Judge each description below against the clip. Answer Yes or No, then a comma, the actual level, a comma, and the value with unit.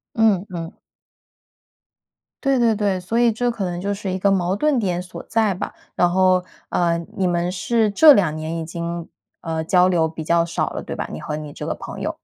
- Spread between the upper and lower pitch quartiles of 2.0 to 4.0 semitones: Yes, average, 3.6 semitones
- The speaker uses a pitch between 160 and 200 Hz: Yes, medium, 185 Hz